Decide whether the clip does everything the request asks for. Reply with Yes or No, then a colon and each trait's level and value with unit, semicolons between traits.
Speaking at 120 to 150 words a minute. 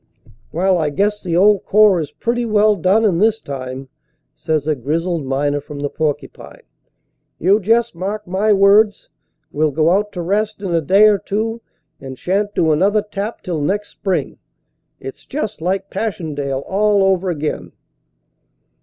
No: average, 170 wpm